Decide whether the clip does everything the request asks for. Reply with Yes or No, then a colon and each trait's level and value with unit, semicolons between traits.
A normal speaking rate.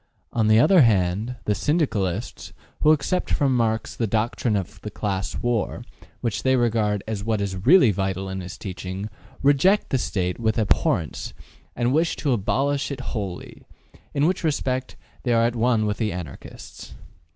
Yes: average, 165 wpm